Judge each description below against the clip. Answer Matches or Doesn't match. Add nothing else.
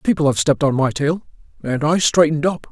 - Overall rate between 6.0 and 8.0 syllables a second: Matches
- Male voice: Matches